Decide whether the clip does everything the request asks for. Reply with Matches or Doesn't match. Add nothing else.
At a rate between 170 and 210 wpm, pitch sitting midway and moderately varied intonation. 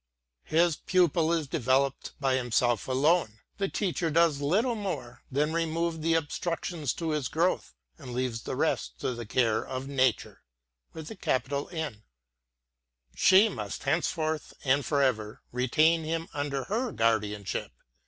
Doesn't match